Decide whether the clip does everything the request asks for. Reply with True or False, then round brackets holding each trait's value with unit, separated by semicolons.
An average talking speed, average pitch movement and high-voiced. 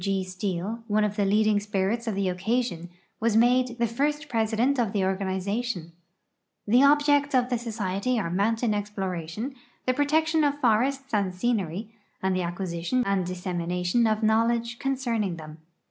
True (160 wpm; 4.5 semitones; 215 Hz)